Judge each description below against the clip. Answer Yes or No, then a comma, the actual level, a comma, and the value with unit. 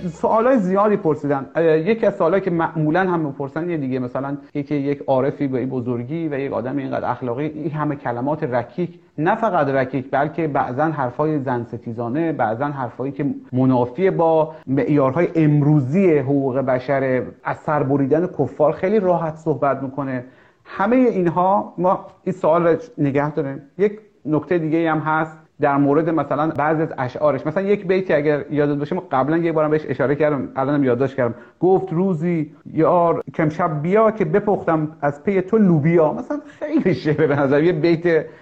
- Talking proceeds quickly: Yes, fast, 165 wpm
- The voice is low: No, medium, 155 Hz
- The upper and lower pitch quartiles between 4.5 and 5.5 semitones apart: No, average, 3.8 semitones